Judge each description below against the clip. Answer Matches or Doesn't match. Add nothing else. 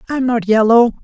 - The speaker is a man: Matches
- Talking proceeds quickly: Doesn't match